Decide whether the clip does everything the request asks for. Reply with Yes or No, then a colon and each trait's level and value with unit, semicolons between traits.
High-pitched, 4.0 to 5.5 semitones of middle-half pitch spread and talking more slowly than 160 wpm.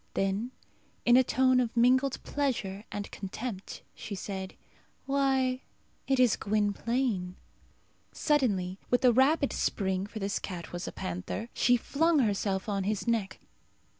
Yes: high, 225 Hz; average, 4.8 semitones; slow, 135 wpm